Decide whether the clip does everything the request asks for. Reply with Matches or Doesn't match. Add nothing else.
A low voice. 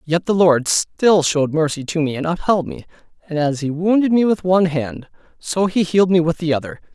Doesn't match